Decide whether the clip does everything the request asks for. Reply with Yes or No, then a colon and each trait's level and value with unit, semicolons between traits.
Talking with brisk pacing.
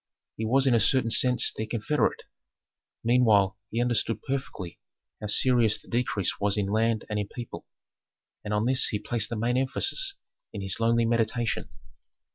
No: average, 165 wpm